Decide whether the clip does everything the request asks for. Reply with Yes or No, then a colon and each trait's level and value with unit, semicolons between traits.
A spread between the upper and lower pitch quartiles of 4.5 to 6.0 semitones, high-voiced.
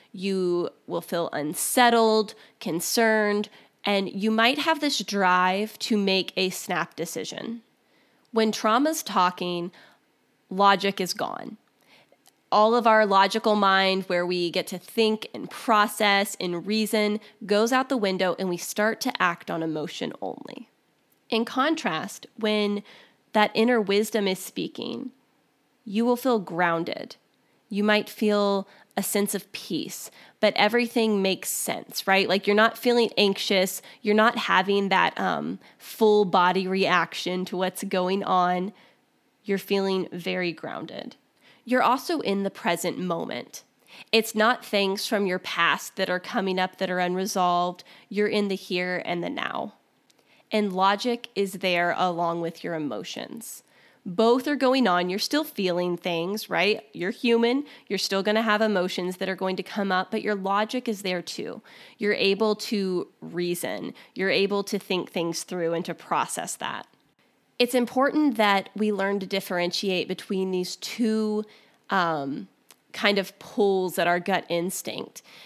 No: average, 3.2 semitones; high, 200 Hz